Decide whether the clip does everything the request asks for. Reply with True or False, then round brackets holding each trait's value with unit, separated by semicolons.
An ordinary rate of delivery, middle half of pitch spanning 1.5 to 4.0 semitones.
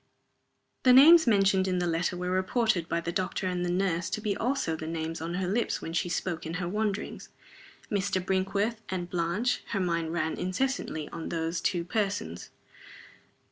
True (180 wpm; 3.2 semitones)